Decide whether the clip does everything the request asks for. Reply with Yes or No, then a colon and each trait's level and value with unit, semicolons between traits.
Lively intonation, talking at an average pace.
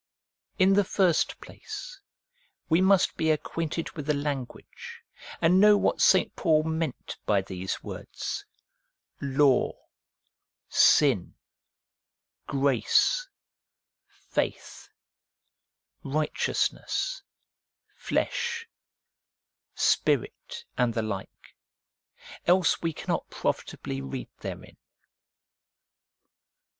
No: wide, 6.4 semitones; slow, 80 wpm